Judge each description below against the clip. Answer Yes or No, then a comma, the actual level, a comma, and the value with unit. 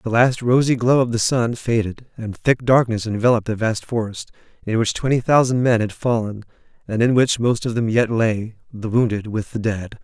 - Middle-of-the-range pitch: No, low, 115 Hz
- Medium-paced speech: No, fast, 210 wpm